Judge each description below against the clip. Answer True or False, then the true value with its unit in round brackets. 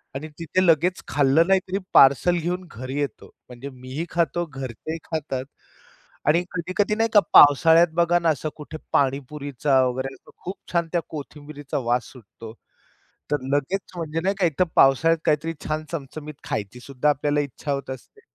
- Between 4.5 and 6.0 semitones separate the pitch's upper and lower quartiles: False (3.9 semitones)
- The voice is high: False (150 Hz)